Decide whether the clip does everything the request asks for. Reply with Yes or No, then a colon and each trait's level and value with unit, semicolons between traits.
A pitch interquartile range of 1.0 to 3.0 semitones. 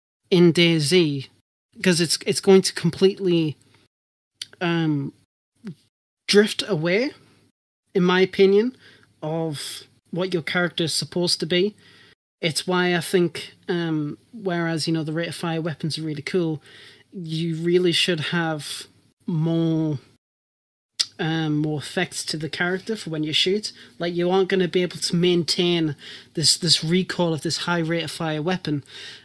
Yes: narrow, 2.6 semitones